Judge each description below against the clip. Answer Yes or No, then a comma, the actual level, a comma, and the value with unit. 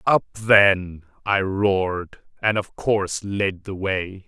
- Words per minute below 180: Yes, average, 140 wpm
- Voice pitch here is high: No, very low, 95 Hz